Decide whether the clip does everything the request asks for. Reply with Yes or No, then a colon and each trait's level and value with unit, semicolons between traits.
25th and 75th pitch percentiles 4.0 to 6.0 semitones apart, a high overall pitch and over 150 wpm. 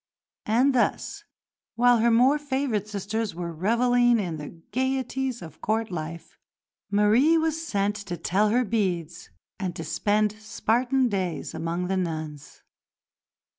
No: wide, 5.5 semitones; high, 215 Hz; slow, 135 wpm